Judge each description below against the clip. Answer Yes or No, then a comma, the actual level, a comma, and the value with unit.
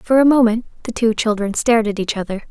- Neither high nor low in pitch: No, high, 225 Hz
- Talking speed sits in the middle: No, fast, 240 wpm